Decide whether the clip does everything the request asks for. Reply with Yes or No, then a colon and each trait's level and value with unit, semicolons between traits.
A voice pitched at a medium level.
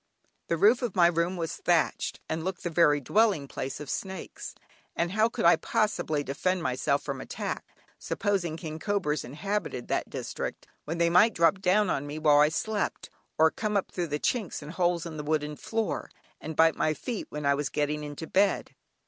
Yes: medium, 165 Hz